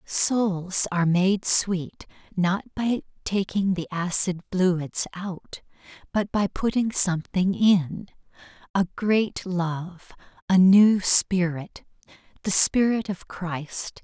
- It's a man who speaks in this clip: No, female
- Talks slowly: Yes, slow, 105 wpm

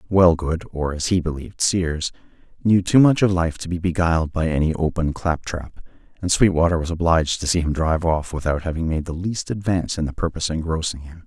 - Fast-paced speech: Yes, fast, 210 wpm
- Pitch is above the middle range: No, very low, 85 Hz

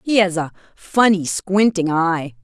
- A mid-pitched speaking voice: Yes, medium, 180 Hz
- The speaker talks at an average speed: Yes, average, 150 wpm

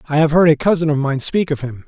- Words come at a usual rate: No, fast, 320 wpm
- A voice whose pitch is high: No, medium, 150 Hz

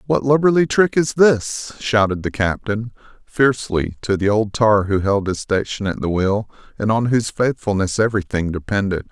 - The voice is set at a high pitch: No, low, 110 Hz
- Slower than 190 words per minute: Yes, average, 170 wpm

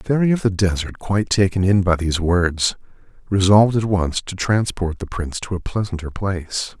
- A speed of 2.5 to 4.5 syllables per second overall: No, 5.5 syllables/s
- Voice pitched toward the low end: Yes, very low, 95 Hz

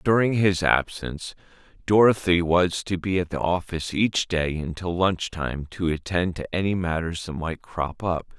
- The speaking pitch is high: No, very low, 90 Hz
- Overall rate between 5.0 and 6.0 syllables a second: No, 4.6 syllables/s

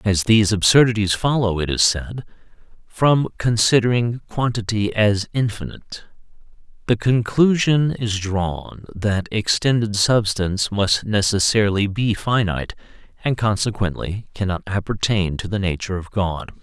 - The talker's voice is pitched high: No, low, 105 Hz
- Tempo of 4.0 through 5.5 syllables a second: Yes, 4.6 syllables/s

